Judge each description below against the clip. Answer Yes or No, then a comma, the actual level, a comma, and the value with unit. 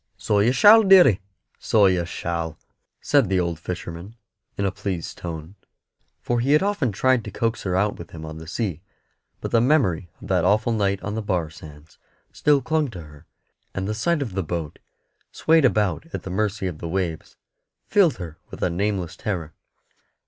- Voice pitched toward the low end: Yes, very low, 95 Hz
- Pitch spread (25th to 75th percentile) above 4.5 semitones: Yes, wide, 5.4 semitones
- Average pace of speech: Yes, average, 190 wpm